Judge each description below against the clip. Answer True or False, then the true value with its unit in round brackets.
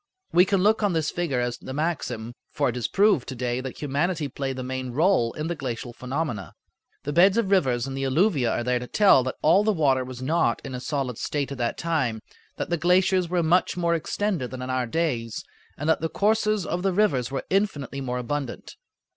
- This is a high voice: False (145 Hz)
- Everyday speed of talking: False (220 wpm)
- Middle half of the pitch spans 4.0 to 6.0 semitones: True (5.6 semitones)